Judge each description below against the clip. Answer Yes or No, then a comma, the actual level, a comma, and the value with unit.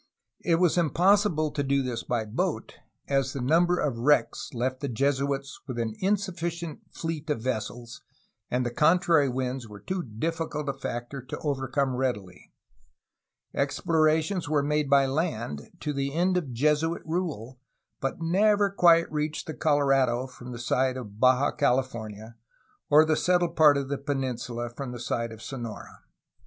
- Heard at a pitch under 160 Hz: Yes, medium, 140 Hz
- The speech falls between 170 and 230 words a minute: No, average, 160 wpm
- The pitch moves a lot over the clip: No, average, 4.4 semitones